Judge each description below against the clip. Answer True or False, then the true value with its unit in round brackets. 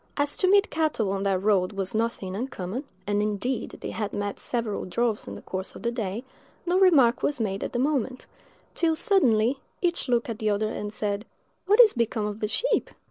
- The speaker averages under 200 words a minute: False (205 wpm)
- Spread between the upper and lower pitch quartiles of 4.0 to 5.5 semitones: True (5.1 semitones)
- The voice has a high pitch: True (225 Hz)